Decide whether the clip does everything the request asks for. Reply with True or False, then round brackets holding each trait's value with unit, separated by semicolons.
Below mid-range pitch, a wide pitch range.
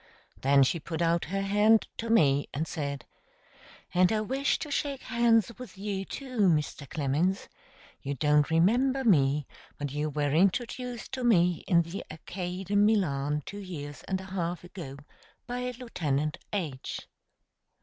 False (180 Hz; 6.6 semitones)